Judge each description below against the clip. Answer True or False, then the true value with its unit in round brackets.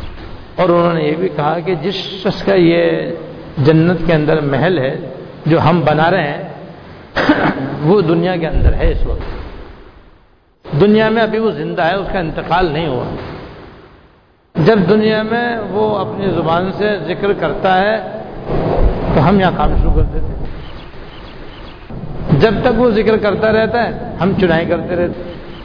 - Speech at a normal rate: False (160 wpm)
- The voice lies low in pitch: False (180 Hz)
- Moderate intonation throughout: True (4.2 semitones)